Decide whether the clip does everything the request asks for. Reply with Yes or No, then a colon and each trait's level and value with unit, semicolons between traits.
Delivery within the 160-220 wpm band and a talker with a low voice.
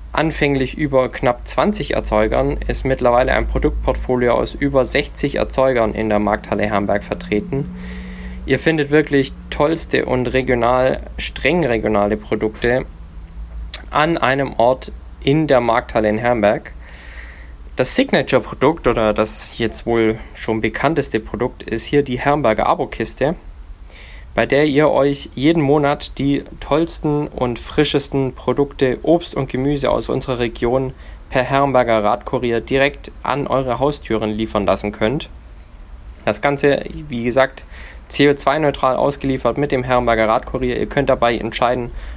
No: average, 130 wpm; low, 120 Hz